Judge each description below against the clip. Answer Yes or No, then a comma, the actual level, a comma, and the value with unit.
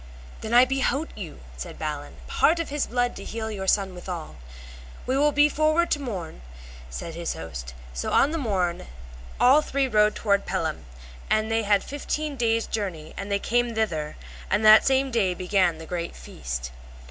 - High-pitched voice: Yes, high, 215 Hz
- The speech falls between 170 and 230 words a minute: Yes, average, 180 wpm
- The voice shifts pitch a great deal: Yes, wide, 7.0 semitones